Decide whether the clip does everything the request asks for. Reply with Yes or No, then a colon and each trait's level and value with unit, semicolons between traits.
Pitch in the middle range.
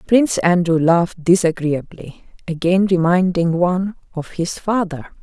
Yes: medium, 175 Hz